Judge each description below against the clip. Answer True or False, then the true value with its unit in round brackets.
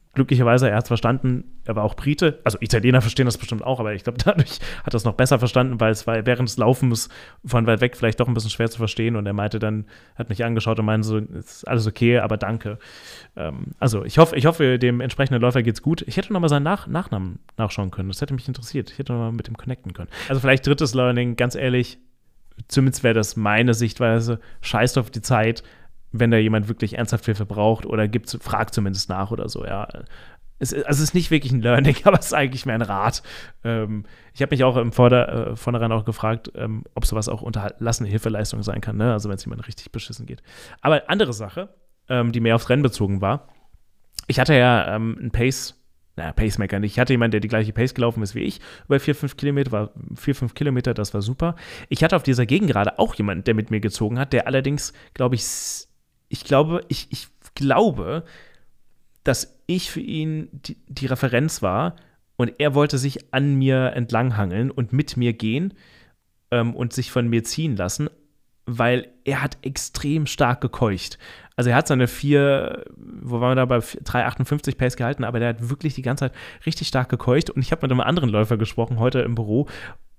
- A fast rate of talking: True (215 wpm)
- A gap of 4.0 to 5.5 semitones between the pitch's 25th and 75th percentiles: False (3.2 semitones)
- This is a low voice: True (120 Hz)